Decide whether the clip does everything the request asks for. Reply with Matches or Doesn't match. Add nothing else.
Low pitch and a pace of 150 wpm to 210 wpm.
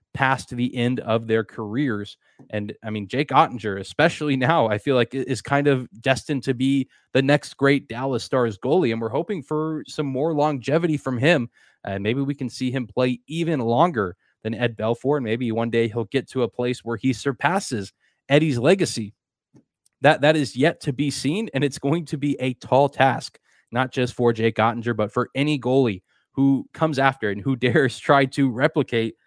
Matches